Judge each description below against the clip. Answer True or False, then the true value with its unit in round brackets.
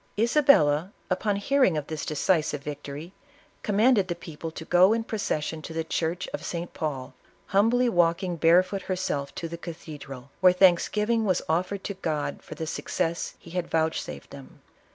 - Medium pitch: True (170 Hz)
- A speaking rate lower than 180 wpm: True (160 wpm)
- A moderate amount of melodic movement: True (4.0 semitones)